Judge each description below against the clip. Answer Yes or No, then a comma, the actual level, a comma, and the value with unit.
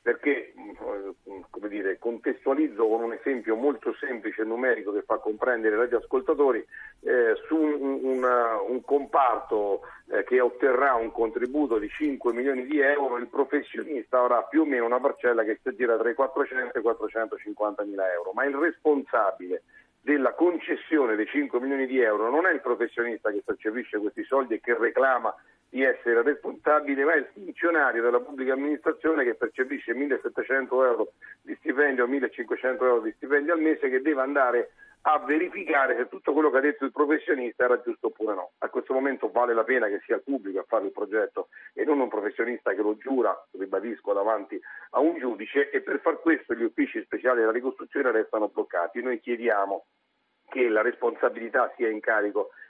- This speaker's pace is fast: Yes, fast, 180 wpm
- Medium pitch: Yes, medium, 150 Hz